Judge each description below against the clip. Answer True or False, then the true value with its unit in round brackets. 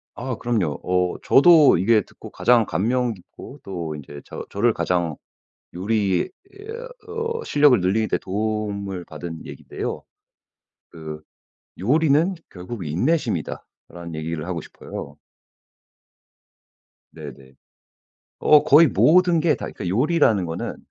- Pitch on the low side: True (105 Hz)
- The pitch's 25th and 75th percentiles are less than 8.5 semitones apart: False (9.0 semitones)